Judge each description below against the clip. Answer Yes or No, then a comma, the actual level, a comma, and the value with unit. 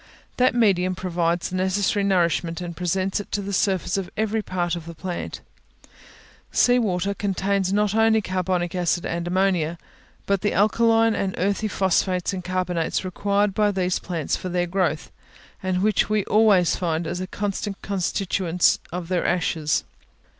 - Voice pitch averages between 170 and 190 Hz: Yes, medium, 185 Hz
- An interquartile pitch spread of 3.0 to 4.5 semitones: No, narrow, 2.4 semitones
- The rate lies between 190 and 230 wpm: No, average, 155 wpm